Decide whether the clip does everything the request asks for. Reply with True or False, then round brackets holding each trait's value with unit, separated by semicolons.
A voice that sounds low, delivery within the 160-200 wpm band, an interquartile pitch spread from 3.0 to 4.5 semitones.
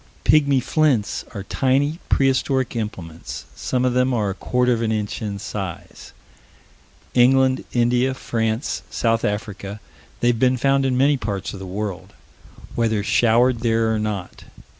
False (115 Hz; 145 wpm; 3.6 semitones)